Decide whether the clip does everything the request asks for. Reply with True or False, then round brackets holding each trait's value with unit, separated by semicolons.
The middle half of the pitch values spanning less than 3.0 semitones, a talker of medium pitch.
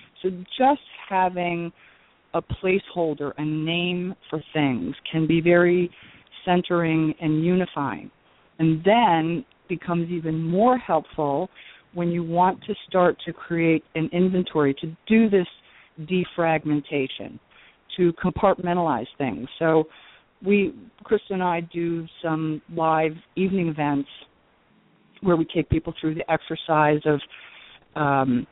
True (2.5 semitones; 170 Hz)